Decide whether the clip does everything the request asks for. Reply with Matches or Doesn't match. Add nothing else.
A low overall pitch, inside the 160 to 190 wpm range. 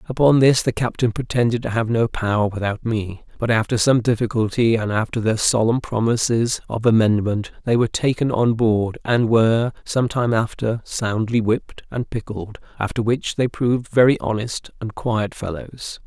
Matches